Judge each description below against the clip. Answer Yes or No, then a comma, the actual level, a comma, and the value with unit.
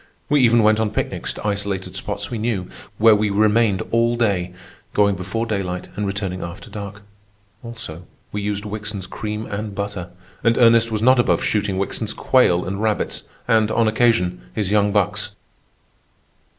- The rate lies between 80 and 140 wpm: No, average, 165 wpm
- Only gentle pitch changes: Yes, narrow, 2.2 semitones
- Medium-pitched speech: No, low, 105 Hz